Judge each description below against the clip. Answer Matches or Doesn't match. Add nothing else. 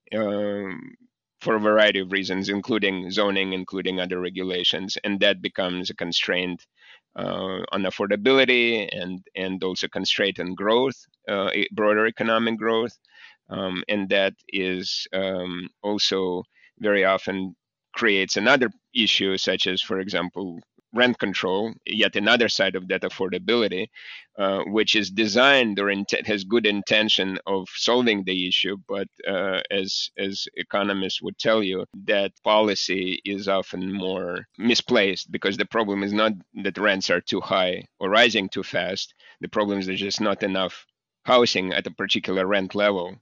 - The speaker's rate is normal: Matches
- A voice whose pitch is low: Matches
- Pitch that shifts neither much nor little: Doesn't match